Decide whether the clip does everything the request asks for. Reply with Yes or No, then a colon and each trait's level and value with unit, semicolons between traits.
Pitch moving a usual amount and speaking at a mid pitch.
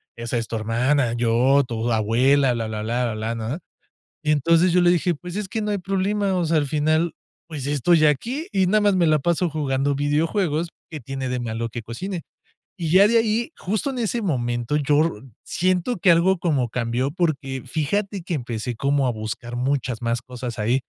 No: wide, 6.7 semitones; medium, 145 Hz